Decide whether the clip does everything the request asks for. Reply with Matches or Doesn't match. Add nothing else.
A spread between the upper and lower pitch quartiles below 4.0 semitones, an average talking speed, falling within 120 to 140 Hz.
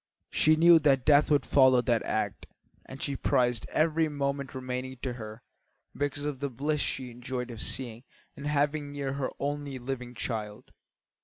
Matches